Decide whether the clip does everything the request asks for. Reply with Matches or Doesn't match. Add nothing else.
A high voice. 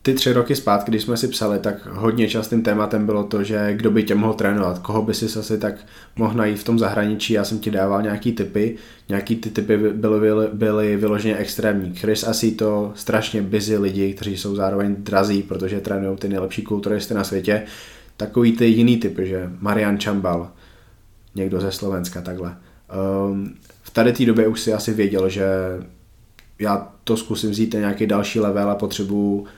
Doesn't match